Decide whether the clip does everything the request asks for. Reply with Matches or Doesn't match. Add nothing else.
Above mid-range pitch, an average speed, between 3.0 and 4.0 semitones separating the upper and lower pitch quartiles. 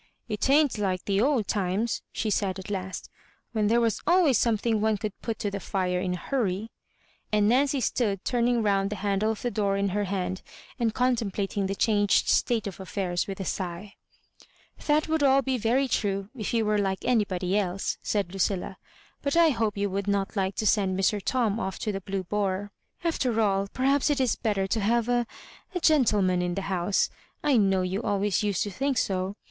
Doesn't match